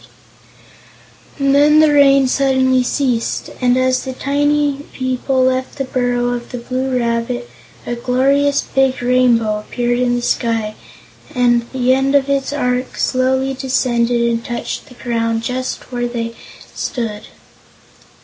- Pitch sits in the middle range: No, very high, 255 Hz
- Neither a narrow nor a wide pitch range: No, narrow, 1.9 semitones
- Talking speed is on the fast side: No, average, 140 wpm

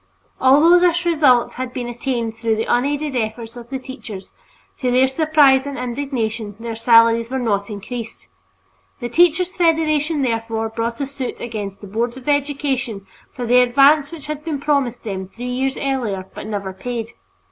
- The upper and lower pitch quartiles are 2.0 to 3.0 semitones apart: No, average, 3.9 semitones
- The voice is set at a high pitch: Yes, very high, 250 Hz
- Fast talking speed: No, average, 170 wpm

